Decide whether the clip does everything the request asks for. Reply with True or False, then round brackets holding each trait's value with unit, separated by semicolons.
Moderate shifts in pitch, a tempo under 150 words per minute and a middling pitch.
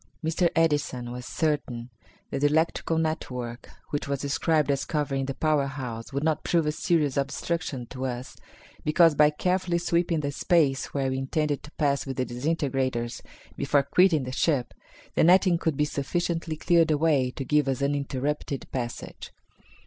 False (3.3 semitones; 165 wpm; 145 Hz)